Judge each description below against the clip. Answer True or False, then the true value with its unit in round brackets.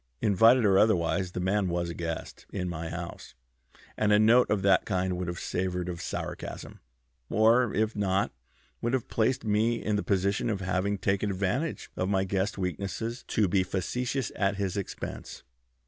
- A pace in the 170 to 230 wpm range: True (175 wpm)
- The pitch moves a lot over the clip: False (2.9 semitones)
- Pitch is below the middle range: True (100 Hz)